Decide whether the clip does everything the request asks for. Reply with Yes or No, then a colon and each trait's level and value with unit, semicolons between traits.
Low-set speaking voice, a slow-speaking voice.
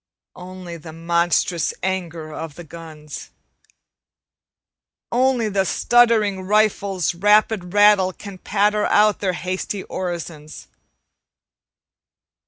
No: medium, 185 Hz; slow, 90 wpm